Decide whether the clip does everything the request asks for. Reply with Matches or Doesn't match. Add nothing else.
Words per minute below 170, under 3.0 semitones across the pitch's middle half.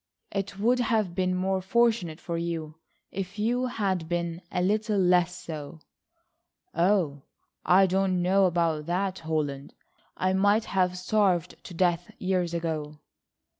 Matches